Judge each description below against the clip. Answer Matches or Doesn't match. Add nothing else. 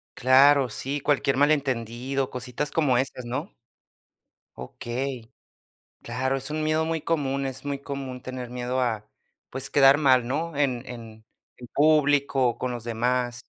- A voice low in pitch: Matches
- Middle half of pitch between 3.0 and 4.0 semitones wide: Doesn't match